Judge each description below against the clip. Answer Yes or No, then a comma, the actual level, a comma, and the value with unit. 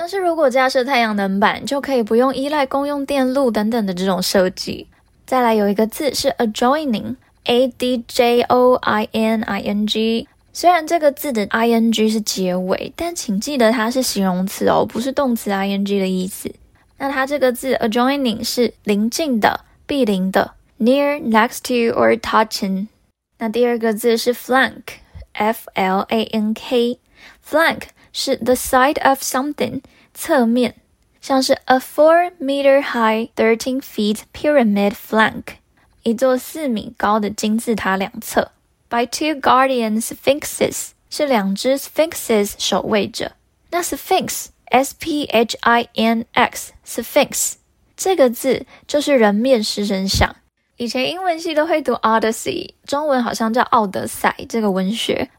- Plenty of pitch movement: No, average, 3.7 semitones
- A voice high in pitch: Yes, high, 240 Hz